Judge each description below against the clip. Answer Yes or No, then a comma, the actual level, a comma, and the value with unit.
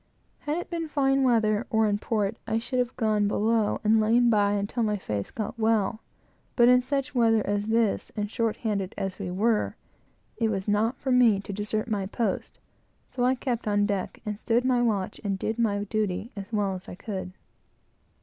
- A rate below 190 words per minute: No, average, 200 wpm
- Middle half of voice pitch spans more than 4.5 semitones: No, narrow, 2.6 semitones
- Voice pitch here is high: Yes, high, 220 Hz